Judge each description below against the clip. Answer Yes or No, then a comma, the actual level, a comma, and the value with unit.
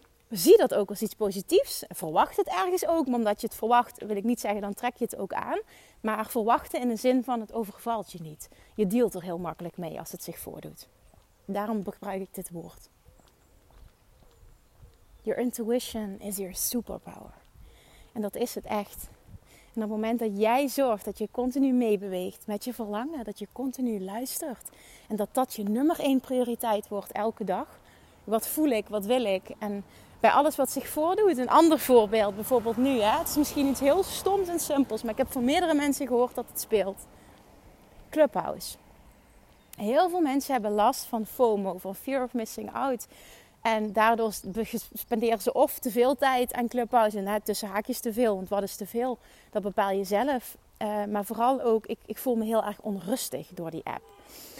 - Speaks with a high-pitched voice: Yes, high, 225 Hz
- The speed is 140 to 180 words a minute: No, average, 195 wpm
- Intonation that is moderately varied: Yes, average, 3.8 semitones